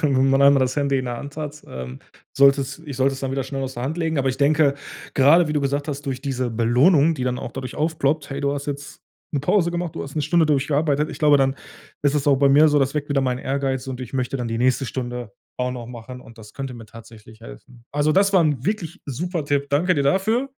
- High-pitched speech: No, medium, 140 Hz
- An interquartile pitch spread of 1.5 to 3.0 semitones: Yes, narrow, 2.6 semitones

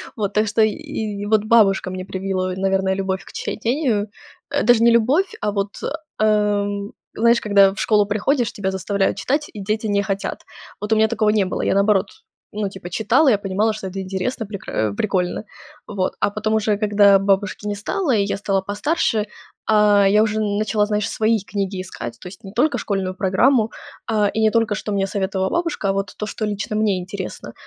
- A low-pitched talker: No, high, 205 Hz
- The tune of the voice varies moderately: No, narrow, 1.9 semitones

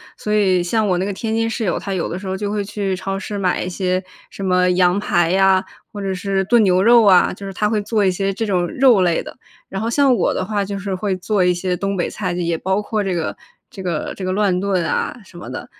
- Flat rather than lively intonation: Yes, narrow, 2.3 semitones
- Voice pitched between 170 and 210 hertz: Yes, high, 195 Hz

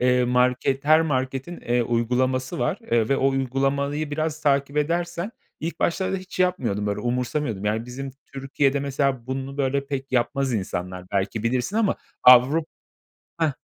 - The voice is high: No, low, 135 Hz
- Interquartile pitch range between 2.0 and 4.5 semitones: Yes, average, 3.1 semitones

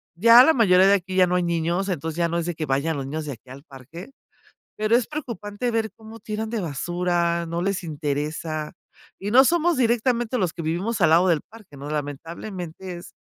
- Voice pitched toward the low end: No, medium, 175 Hz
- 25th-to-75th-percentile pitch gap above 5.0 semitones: Yes, wide, 5.4 semitones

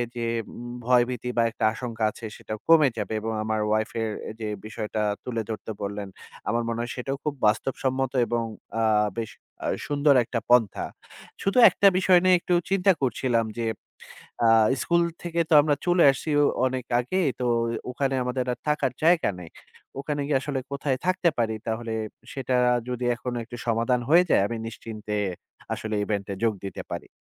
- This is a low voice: Yes, low, 125 Hz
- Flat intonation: No, average, 4.2 semitones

